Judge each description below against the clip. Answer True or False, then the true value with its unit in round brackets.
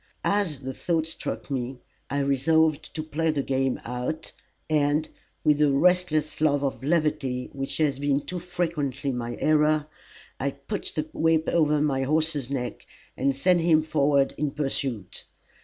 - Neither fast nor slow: True (155 wpm)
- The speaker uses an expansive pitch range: False (2.6 semitones)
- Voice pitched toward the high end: False (145 Hz)